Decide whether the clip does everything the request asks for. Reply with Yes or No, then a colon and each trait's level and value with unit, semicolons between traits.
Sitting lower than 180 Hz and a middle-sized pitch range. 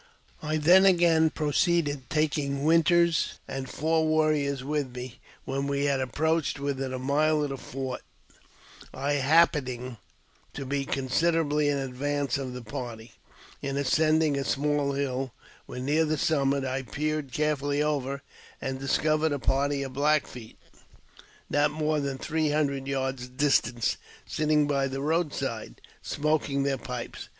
No: medium, 140 Hz; narrow, 2.3 semitones